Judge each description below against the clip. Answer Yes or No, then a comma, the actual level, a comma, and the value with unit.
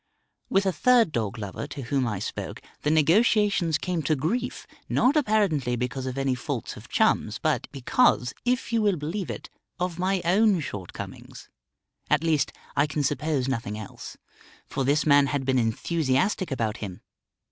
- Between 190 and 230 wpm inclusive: No, average, 165 wpm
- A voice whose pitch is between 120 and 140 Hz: No, medium, 150 Hz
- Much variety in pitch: Yes, wide, 6.8 semitones